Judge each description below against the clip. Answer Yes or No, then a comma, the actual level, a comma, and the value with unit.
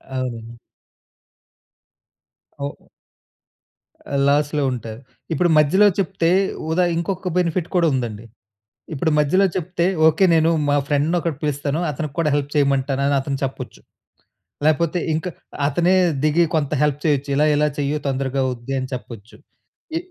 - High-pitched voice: No, medium, 145 Hz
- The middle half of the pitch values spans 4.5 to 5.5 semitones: No, average, 3.3 semitones